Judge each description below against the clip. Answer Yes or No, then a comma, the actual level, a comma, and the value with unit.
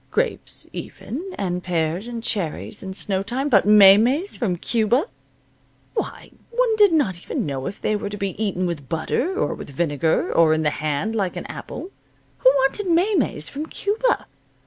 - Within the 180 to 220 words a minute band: No, average, 170 wpm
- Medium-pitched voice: No, high, 205 Hz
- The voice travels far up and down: Yes, wide, 8.7 semitones